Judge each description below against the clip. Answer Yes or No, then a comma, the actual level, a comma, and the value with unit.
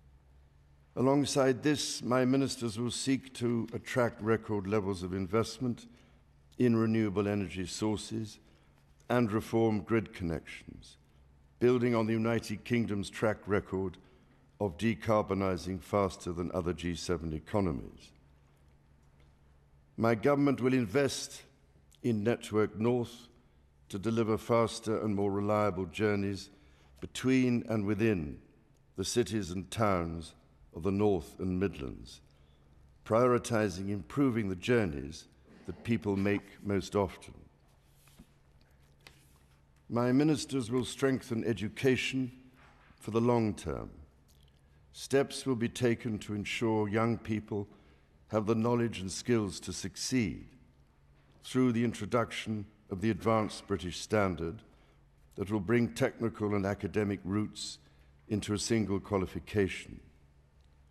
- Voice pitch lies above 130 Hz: No, low, 105 Hz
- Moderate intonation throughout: No, wide, 6.3 semitones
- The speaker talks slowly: Yes, slow, 110 wpm